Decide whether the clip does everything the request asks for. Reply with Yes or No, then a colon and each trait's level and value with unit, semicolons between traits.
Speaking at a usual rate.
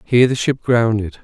Yes: average, 195 wpm